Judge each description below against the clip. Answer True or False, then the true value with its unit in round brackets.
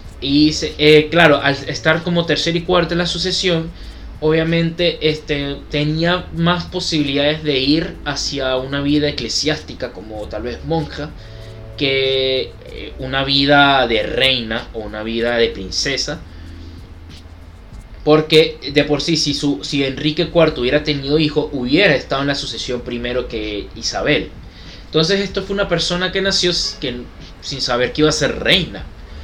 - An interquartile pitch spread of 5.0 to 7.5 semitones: True (5.6 semitones)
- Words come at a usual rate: True (150 wpm)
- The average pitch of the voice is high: False (140 Hz)